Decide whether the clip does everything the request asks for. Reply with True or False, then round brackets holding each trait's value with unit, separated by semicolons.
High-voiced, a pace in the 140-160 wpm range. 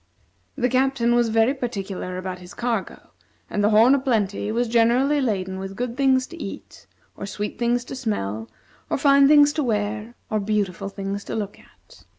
False (225 Hz; 180 wpm)